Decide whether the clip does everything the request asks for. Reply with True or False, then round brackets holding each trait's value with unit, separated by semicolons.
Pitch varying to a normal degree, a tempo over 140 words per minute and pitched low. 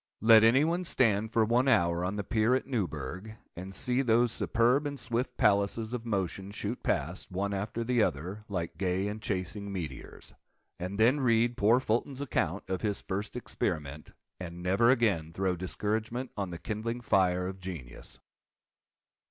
True (4.2 semitones; 160 wpm; 105 Hz)